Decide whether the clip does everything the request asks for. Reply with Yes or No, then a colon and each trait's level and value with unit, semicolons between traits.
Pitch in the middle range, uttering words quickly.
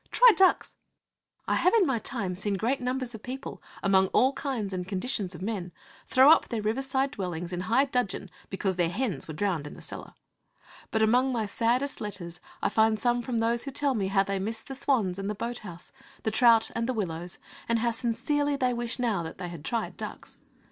No: high, 225 Hz; fast, 210 wpm